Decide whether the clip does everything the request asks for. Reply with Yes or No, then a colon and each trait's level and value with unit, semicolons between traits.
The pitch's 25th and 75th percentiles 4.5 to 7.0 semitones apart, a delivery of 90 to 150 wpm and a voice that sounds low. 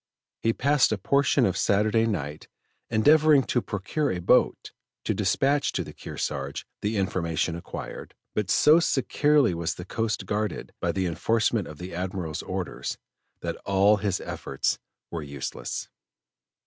Yes: wide, 5.4 semitones; average, 145 wpm; low, 100 Hz